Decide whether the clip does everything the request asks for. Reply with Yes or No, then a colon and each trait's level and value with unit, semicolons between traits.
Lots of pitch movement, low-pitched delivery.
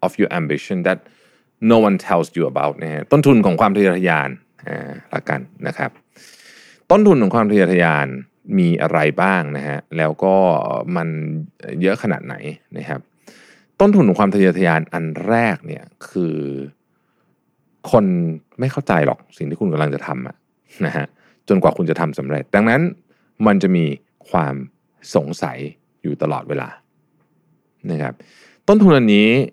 Yes: wide, 5.8 semitones; very low, 85 Hz